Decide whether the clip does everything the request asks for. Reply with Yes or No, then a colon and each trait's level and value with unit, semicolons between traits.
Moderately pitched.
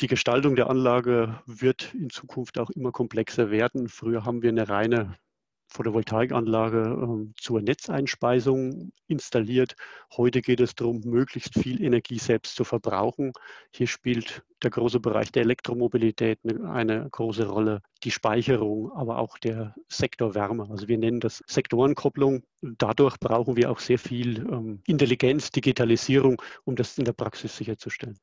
No: low, 120 Hz